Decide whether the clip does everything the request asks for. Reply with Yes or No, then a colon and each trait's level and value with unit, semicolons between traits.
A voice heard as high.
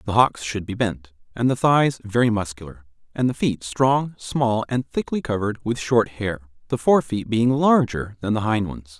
No: low, 115 Hz